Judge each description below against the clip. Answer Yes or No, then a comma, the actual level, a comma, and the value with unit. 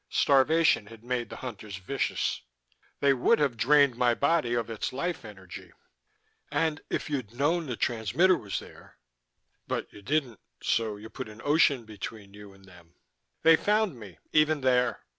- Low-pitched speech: Yes, low, 120 Hz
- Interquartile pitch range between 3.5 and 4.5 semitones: No, wide, 5.5 semitones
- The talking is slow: No, average, 160 wpm